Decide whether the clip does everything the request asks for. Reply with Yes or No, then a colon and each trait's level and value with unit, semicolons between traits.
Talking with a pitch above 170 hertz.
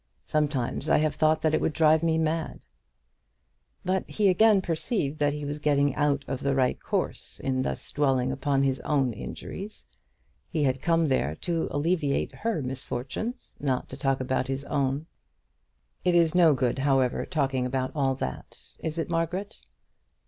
No: medium, 145 Hz